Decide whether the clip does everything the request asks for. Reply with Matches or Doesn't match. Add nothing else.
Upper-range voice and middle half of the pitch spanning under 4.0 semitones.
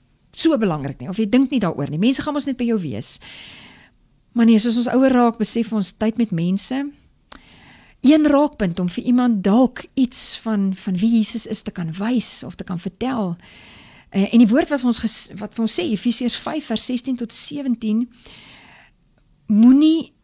Matches